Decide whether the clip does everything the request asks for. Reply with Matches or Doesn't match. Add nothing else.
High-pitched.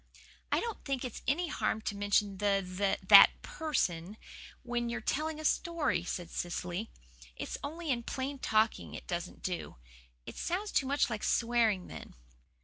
Matches